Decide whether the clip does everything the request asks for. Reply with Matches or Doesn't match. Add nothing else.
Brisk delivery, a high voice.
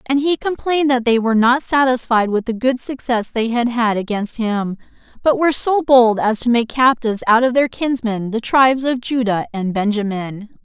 Doesn't match